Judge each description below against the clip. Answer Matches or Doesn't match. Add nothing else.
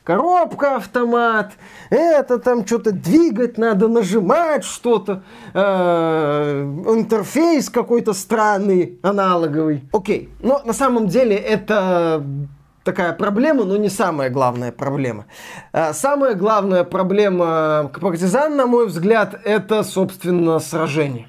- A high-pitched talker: Matches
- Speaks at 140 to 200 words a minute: Doesn't match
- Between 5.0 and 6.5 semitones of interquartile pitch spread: Matches